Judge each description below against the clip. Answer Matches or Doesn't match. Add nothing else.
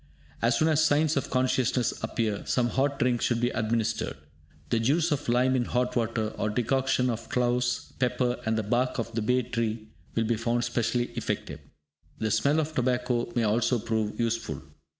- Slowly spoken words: Doesn't match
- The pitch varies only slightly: Matches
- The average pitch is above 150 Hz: Doesn't match